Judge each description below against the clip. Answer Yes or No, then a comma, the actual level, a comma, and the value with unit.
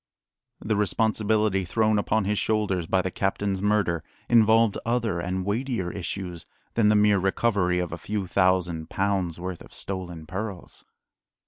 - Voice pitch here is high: No, low, 100 Hz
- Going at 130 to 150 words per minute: Yes, average, 145 wpm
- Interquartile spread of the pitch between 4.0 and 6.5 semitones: No, average, 2.9 semitones